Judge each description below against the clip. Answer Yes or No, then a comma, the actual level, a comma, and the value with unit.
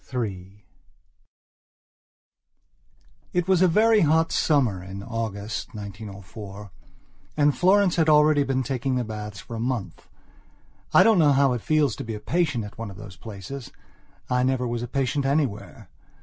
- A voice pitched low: Yes, low, 125 Hz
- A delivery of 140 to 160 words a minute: Yes, average, 155 wpm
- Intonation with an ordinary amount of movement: No, wide, 6.0 semitones